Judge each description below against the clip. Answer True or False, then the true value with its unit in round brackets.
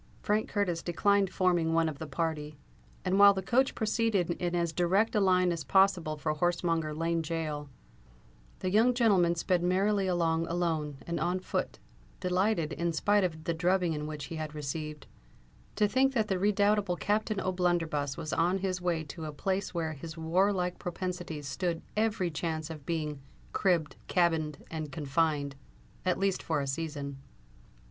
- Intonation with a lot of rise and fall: False (3.3 semitones)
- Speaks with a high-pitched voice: False (170 Hz)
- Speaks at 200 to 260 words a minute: False (165 wpm)